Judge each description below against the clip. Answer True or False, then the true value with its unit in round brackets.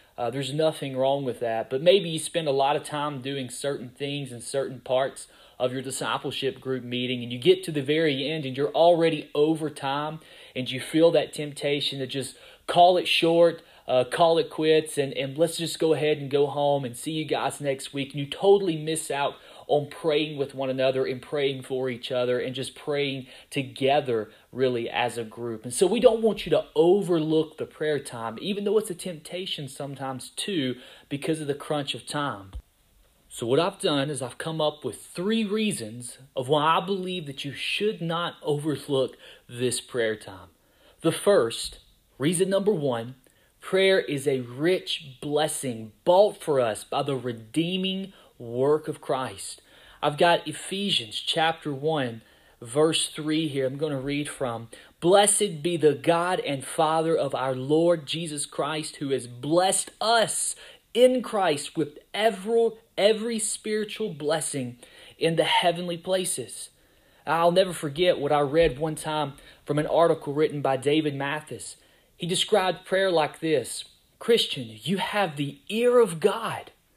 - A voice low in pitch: False (150 Hz)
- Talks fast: False (170 wpm)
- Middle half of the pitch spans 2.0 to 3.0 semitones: False (4.2 semitones)